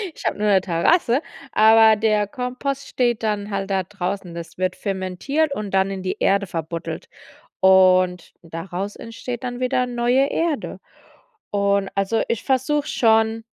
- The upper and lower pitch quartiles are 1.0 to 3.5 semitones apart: No, average, 4.4 semitones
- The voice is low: No, high, 210 Hz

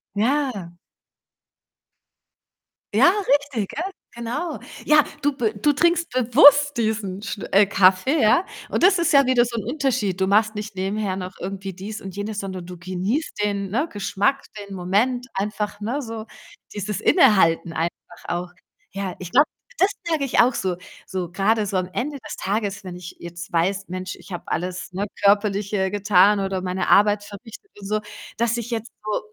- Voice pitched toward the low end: No, high, 205 Hz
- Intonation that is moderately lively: Yes, average, 4.1 semitones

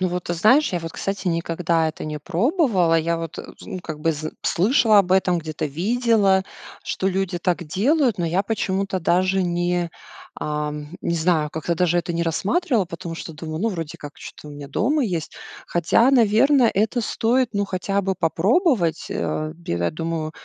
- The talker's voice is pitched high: No, medium, 180 Hz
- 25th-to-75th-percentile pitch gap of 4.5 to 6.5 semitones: No, average, 3.7 semitones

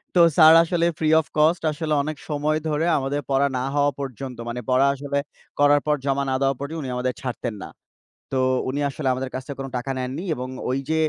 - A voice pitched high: No, medium, 140 Hz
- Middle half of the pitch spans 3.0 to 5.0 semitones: No, narrow, 2.4 semitones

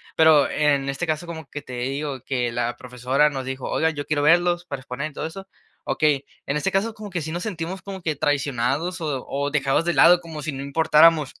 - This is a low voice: No, medium, 150 Hz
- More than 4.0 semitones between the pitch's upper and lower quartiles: No, average, 3.5 semitones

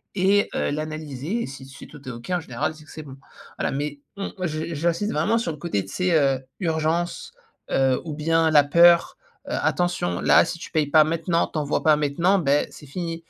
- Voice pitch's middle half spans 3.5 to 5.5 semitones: No, average, 2.9 semitones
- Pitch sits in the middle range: Yes, medium, 155 Hz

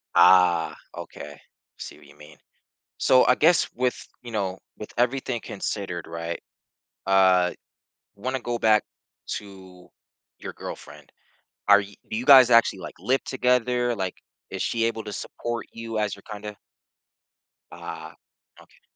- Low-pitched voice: Yes, low, 105 Hz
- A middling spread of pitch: Yes, average, 4.3 semitones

